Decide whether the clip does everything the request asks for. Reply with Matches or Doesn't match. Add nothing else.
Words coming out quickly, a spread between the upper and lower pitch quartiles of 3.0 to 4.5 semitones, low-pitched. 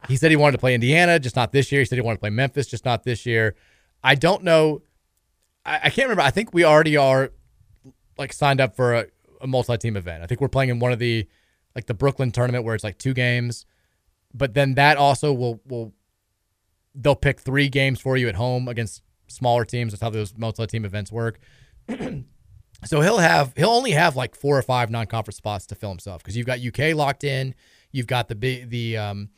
Matches